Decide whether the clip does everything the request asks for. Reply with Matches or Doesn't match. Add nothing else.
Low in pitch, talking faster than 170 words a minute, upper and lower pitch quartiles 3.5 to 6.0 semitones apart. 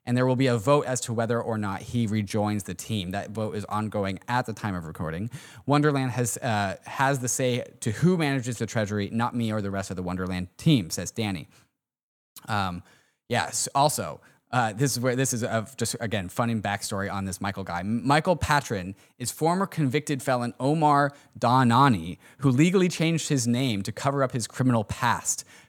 Matches